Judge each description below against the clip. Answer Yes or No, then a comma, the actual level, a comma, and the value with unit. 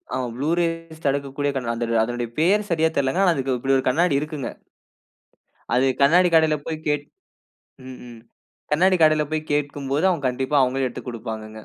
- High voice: No, medium, 145 Hz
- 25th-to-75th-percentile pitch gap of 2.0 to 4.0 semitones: Yes, average, 3.6 semitones